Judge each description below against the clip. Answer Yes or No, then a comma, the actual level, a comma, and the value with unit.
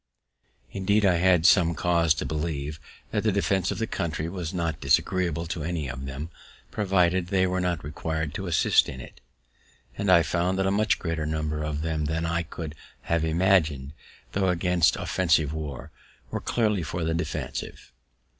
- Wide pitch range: No, average, 3.0 semitones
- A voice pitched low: Yes, very low, 85 Hz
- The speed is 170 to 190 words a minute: Yes, average, 175 wpm